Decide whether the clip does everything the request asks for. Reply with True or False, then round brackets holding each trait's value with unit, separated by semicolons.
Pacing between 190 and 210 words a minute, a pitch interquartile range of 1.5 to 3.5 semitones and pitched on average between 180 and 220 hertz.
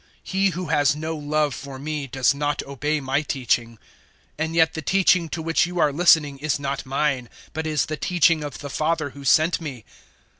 False (200 wpm; 2.5 semitones; 150 Hz)